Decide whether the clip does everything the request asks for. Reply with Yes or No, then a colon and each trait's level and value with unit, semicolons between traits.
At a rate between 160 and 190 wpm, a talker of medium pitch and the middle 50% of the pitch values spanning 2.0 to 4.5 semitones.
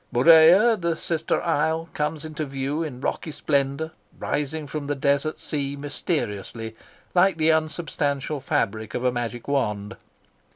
No: slow, 135 wpm; medium, 145 Hz; average, 2.9 semitones